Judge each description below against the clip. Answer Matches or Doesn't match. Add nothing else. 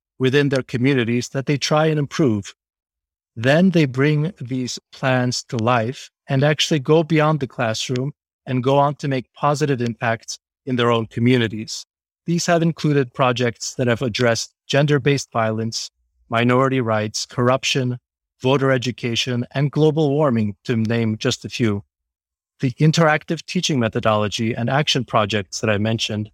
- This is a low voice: Matches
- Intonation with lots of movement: Doesn't match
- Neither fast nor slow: Matches